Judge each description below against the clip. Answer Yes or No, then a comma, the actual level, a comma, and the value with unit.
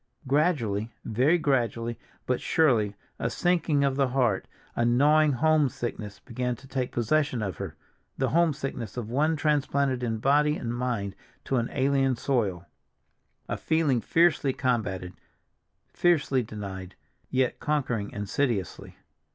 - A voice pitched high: No, low, 130 Hz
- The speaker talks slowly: Yes, slow, 125 wpm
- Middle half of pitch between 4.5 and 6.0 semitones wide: No, average, 4.0 semitones